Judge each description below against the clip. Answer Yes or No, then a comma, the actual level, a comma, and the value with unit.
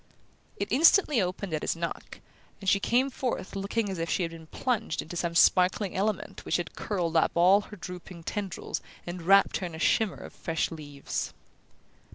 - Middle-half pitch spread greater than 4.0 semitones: No, average, 3.5 semitones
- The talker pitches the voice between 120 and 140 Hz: No, medium, 185 Hz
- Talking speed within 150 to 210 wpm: Yes, average, 190 wpm